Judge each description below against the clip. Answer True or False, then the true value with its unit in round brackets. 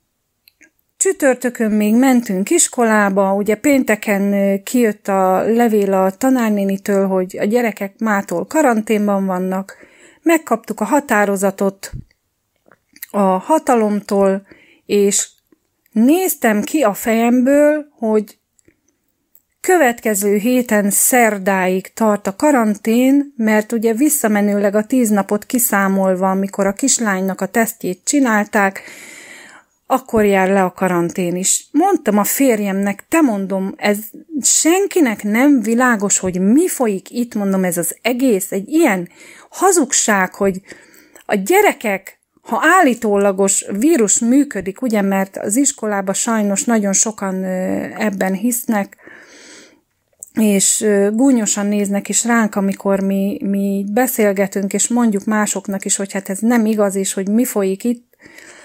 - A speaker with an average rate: False (115 wpm)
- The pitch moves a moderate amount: True (3.9 semitones)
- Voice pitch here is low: False (210 Hz)